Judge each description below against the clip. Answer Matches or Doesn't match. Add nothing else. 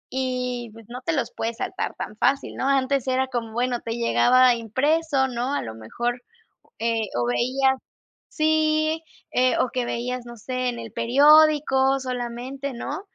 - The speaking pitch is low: Doesn't match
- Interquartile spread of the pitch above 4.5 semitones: Doesn't match